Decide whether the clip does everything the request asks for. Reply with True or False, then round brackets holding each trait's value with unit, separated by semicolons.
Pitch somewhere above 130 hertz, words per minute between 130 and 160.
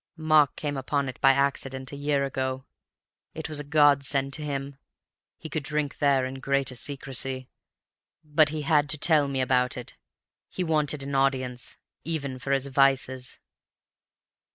True (140 Hz; 155 wpm)